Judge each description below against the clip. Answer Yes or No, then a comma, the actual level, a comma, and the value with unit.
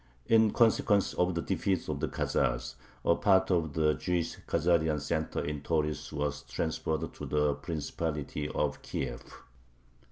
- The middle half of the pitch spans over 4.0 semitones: No, average, 2.8 semitones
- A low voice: Yes, very low, 80 Hz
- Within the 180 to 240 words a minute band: No, average, 140 wpm